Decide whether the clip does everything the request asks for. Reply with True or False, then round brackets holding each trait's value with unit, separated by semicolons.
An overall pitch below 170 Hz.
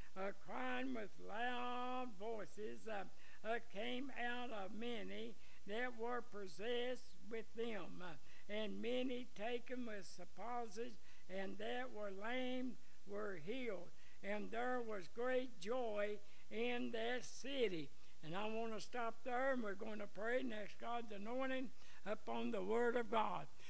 False (230 Hz)